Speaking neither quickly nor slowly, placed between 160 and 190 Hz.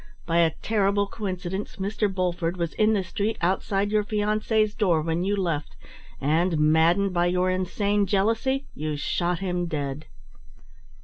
Yes: average, 145 wpm; medium, 185 Hz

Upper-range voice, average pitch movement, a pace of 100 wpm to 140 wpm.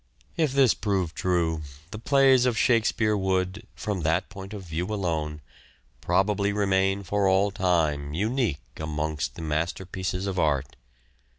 No: very low, 95 Hz; average, 4.3 semitones; slow, 135 wpm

